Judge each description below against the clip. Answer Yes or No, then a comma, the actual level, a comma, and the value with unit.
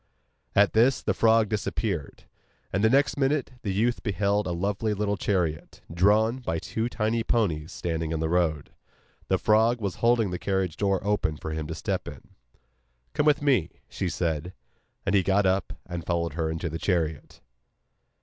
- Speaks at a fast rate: No, average, 175 wpm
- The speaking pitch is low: Yes, low, 100 Hz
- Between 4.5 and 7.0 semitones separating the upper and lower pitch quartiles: Yes, average, 4.8 semitones